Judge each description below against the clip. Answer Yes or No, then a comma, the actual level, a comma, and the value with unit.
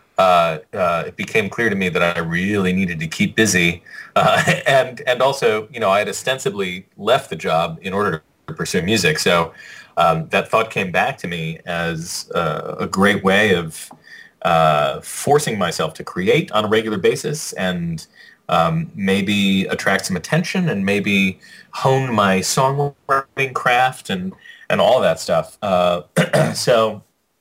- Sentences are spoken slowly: No, average, 160 wpm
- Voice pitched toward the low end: Yes, low, 100 Hz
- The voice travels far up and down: Yes, wide, 7.0 semitones